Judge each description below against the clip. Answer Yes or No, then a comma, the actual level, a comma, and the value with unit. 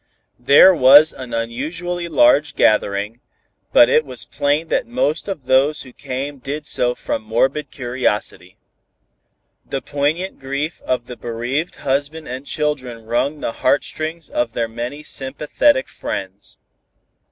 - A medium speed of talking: No, slow, 130 wpm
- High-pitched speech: No, medium, 140 Hz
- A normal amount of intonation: Yes, average, 3.8 semitones